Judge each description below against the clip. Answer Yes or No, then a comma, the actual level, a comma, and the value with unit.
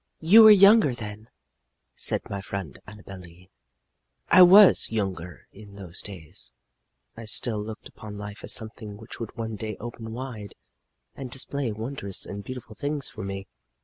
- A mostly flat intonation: No, average, 4.0 semitones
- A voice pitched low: Yes, low, 110 Hz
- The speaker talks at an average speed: Yes, average, 160 wpm